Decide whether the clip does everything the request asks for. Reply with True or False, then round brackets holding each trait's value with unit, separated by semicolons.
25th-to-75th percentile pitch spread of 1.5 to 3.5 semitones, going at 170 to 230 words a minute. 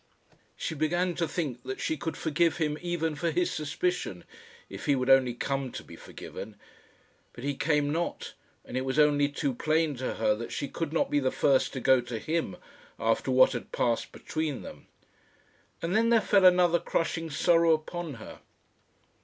False (4.0 semitones; 185 wpm)